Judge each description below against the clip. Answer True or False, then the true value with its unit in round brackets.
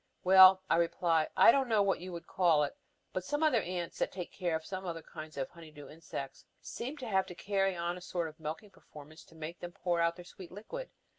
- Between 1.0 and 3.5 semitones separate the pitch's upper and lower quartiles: True (2.8 semitones)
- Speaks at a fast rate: True (240 wpm)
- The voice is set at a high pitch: False (175 Hz)